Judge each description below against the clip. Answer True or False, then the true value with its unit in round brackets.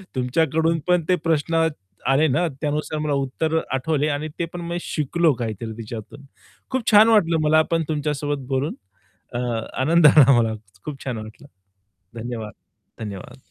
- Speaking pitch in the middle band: True (150 Hz)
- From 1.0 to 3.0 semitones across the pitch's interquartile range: False (3.9 semitones)